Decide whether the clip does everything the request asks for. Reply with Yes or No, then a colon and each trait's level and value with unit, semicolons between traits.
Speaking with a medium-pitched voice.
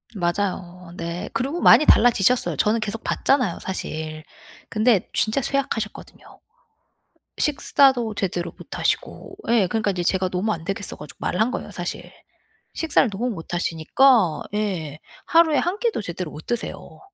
No: high, 210 Hz